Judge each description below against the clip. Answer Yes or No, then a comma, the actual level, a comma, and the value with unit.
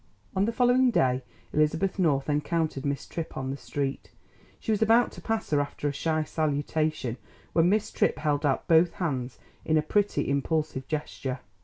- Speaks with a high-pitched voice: No, medium, 155 Hz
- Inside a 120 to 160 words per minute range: No, average, 175 wpm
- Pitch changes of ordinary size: Yes, average, 4.0 semitones